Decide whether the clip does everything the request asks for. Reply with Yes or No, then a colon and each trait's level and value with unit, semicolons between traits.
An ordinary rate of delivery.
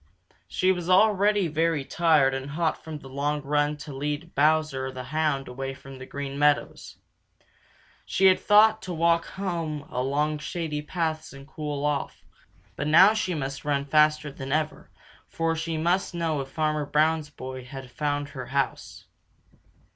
Yes: average, 160 wpm